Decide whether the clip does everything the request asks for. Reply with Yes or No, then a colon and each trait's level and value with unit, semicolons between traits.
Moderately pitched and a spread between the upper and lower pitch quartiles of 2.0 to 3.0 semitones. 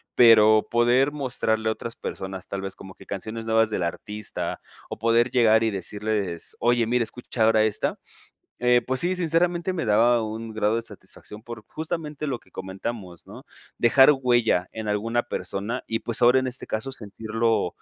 No: low, 115 Hz; narrow, 2.4 semitones